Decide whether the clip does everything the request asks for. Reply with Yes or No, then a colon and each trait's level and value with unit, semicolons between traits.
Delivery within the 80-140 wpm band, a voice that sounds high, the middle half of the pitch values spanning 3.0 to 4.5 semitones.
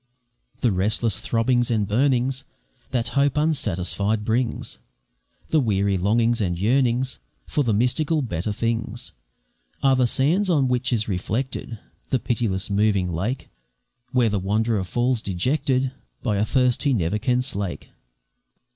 No: slow, 135 wpm; low, 115 Hz; average, 4.0 semitones